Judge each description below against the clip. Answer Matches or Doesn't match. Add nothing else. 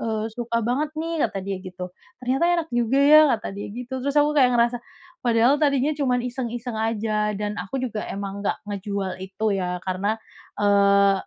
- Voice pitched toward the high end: Matches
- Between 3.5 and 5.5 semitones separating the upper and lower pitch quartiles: Matches